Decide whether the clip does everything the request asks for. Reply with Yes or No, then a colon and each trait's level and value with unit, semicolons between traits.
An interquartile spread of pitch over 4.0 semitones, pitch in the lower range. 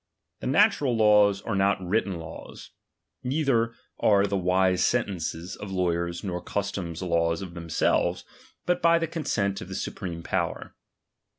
Yes: average, 4.6 semitones; low, 100 Hz